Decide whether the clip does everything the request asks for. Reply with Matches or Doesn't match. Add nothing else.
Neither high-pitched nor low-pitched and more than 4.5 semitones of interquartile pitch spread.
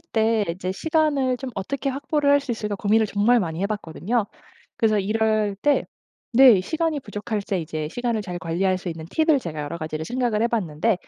Doesn't match